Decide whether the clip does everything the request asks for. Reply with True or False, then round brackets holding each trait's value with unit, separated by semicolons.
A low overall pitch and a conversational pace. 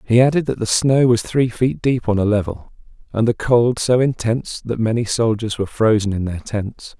False (115 Hz; 215 wpm)